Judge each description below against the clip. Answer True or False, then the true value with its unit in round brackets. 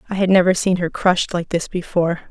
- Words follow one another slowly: False (235 wpm)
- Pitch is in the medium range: True (180 Hz)